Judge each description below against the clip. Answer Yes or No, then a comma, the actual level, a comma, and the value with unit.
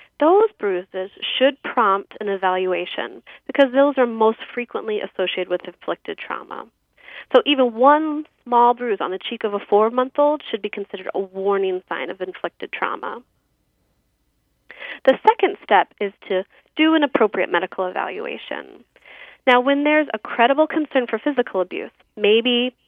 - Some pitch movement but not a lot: No, wide, 6.1 semitones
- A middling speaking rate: Yes, average, 150 wpm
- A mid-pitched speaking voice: No, high, 235 Hz